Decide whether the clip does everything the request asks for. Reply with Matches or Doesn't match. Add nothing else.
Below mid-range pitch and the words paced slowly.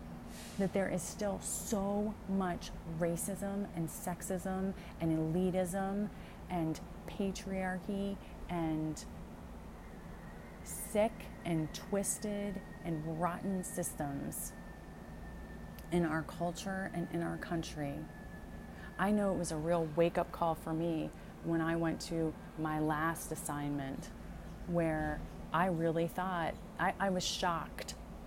Doesn't match